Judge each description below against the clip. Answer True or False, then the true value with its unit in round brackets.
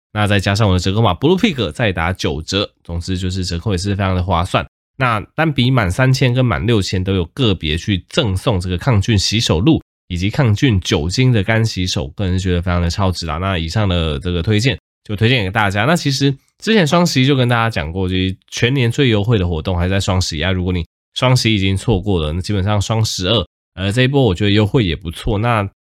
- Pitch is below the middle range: True (100 Hz)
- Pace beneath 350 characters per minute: False (355 characters per minute)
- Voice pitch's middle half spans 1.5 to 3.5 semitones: False (4.4 semitones)